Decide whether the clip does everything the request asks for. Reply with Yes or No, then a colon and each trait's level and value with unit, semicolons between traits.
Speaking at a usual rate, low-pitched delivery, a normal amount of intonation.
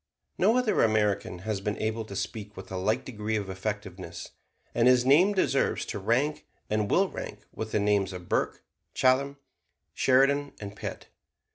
Yes: average, 165 wpm; low, 110 Hz; average, 4.6 semitones